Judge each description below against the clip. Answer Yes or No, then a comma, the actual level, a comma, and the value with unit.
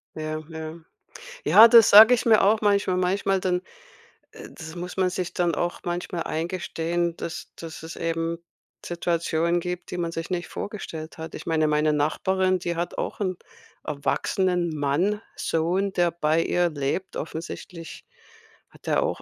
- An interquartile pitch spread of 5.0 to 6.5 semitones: No, narrow, 2.4 semitones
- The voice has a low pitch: No, medium, 175 Hz